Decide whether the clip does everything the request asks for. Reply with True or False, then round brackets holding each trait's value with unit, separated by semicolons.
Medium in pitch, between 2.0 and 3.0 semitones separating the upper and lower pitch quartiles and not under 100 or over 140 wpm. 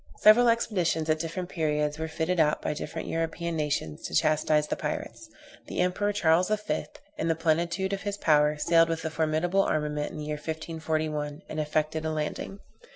False (160 Hz; 2.4 semitones; 180 wpm)